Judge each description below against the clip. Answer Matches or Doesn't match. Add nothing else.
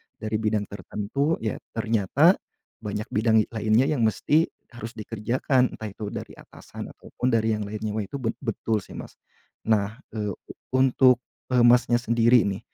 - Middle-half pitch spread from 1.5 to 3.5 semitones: Matches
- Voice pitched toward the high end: Doesn't match